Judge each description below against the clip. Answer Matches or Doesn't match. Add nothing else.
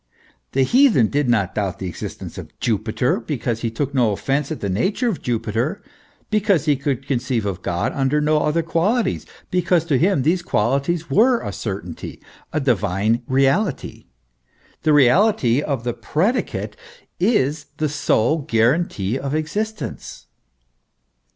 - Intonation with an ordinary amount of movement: Doesn't match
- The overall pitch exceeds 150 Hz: Doesn't match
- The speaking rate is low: Doesn't match